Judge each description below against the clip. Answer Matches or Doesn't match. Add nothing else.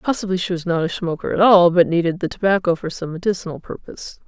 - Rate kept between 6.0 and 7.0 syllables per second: Matches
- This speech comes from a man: Doesn't match